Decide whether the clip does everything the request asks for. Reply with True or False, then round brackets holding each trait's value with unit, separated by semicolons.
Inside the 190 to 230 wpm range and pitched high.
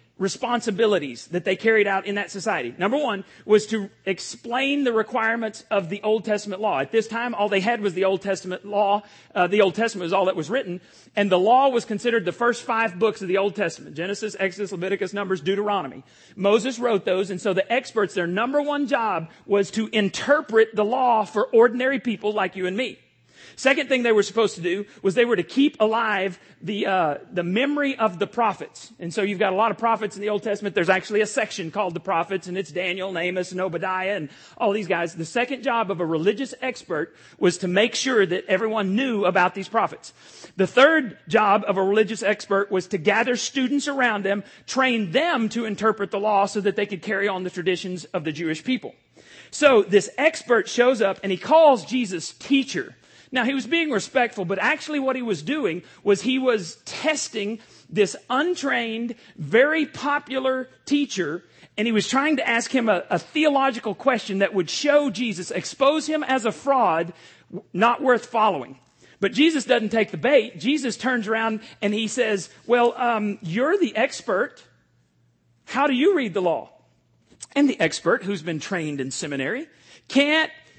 True (195 wpm; 210 Hz)